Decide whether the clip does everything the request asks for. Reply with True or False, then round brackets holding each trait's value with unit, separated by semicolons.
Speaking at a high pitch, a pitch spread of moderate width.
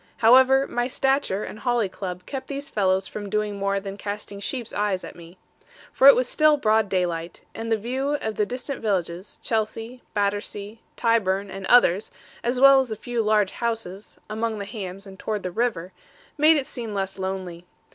True (210 Hz; 4.0 semitones)